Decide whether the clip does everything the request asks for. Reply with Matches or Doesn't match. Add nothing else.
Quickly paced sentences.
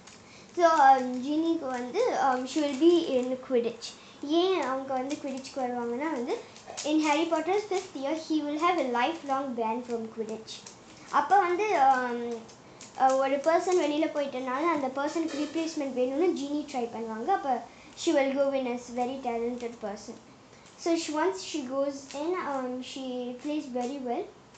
Matches